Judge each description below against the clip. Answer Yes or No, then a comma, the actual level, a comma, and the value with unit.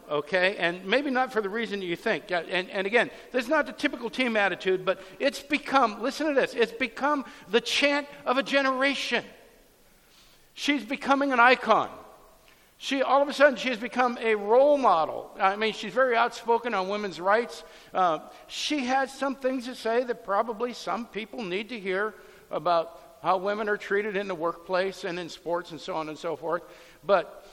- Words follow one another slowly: No, average, 190 wpm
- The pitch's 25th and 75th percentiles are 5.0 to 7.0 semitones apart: Yes, wide, 5.6 semitones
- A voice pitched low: No, high, 225 Hz